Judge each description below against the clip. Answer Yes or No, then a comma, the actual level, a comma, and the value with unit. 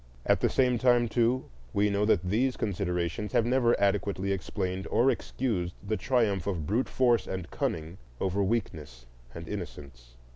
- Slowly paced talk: No, average, 155 wpm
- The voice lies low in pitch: Yes, low, 100 Hz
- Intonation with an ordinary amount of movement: Yes, average, 4.9 semitones